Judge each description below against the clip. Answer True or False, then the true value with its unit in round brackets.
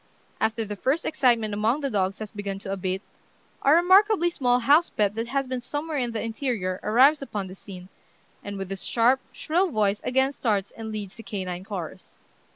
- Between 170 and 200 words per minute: True (190 wpm)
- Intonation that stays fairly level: False (5.3 semitones)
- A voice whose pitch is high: True (225 Hz)